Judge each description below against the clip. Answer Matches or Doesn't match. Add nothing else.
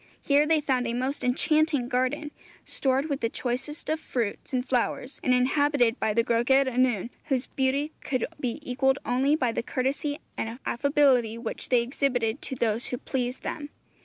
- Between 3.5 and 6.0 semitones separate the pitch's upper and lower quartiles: Doesn't match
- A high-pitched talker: Matches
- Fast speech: Doesn't match